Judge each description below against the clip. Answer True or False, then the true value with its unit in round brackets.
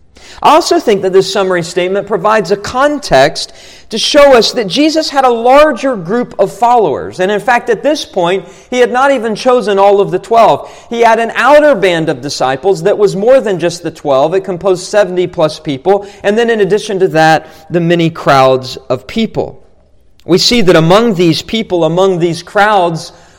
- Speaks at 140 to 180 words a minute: False (190 wpm)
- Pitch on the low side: False (200 Hz)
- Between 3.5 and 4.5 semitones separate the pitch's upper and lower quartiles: False (5.3 semitones)